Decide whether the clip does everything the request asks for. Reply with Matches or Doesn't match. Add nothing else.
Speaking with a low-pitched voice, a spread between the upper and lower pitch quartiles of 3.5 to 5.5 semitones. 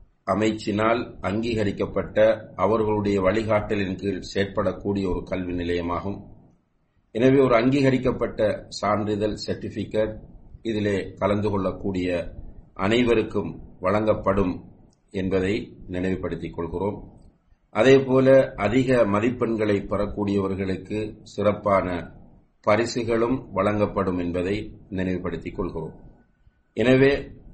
Doesn't match